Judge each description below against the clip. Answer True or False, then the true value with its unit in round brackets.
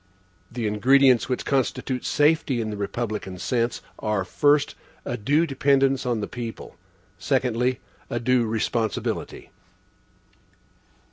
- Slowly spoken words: True (115 wpm)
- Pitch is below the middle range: True (125 Hz)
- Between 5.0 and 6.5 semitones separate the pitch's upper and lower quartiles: False (3.5 semitones)